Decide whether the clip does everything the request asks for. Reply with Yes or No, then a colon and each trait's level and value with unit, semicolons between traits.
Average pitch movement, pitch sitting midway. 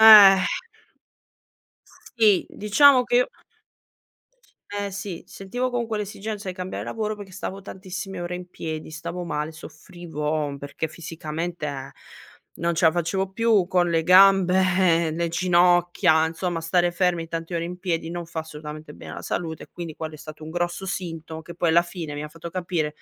Yes: average, 3.0 semitones; medium, 175 Hz